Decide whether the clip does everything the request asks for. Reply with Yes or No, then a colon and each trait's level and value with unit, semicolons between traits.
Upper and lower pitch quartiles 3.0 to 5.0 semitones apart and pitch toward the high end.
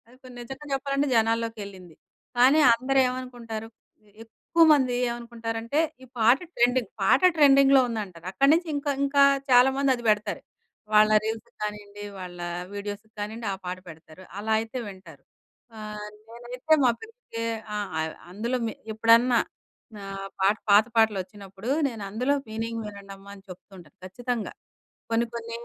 Yes: average, 3.7 semitones; high, 225 Hz